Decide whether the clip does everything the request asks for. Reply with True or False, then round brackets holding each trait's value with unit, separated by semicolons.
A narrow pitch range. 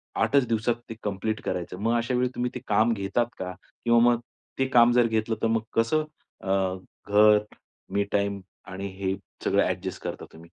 False (3.1 semitones)